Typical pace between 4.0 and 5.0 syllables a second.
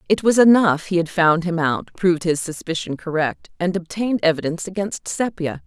No: 5.4 syllables/s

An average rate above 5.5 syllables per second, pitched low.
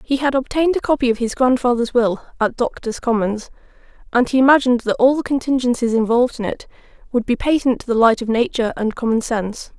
No: 6.3 syllables/s; high, 245 Hz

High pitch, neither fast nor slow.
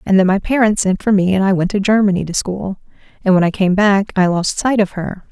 No: high, 195 Hz; fast, 270 wpm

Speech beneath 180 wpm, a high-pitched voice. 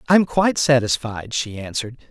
No: average, 140 wpm; low, 130 Hz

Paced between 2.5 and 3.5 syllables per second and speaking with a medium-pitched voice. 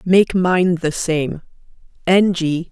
Yes: 3.1 syllables/s; medium, 175 Hz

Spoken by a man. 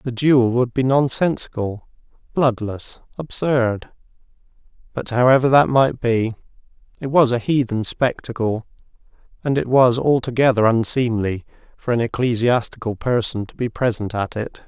Yes: male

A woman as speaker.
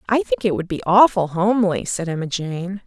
Yes: female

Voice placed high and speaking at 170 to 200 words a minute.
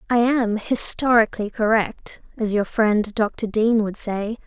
No: high, 220 Hz; average, 150 wpm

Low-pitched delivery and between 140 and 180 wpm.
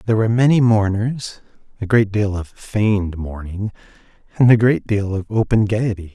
Yes: low, 105 Hz; average, 165 wpm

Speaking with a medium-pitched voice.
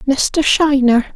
No: very high, 275 Hz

